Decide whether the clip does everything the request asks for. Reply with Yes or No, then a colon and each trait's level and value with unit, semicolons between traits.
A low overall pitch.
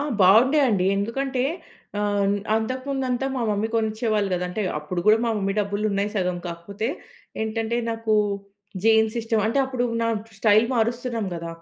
No: high, 220 Hz